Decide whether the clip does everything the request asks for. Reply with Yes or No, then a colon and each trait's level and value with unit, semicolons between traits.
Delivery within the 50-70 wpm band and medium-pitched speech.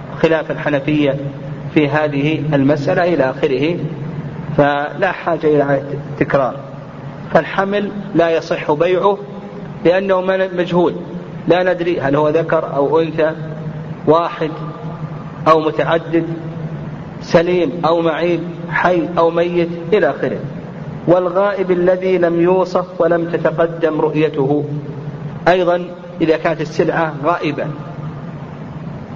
No: average, 95 wpm; medium, 160 Hz